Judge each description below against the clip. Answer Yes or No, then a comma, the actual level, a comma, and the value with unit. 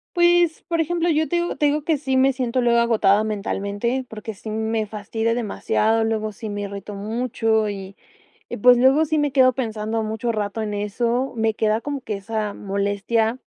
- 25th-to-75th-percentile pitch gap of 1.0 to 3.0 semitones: No, average, 3.6 semitones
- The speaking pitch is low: No, high, 225 Hz